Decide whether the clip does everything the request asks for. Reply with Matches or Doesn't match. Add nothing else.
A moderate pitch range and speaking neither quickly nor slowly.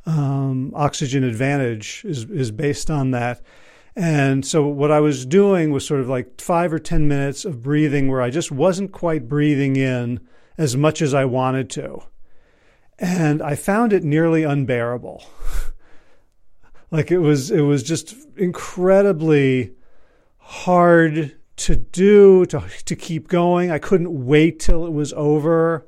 Matches